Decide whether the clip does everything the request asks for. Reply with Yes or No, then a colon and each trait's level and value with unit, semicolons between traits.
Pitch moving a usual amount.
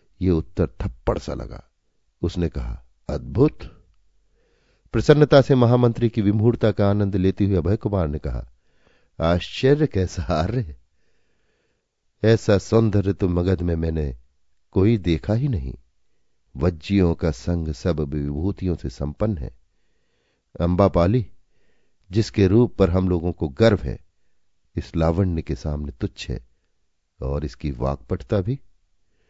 Yes: average, 5.0 semitones